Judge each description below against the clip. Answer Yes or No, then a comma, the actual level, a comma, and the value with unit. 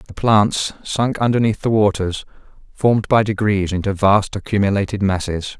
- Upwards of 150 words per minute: No, average, 140 wpm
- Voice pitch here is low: Yes, low, 100 Hz